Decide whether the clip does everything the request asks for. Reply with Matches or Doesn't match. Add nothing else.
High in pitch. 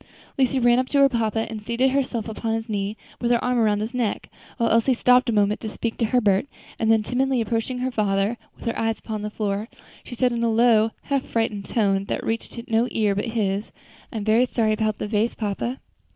Matches